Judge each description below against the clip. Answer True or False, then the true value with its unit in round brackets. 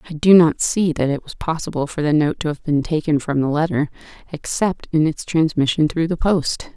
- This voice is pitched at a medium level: True (155 Hz)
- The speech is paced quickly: True (220 wpm)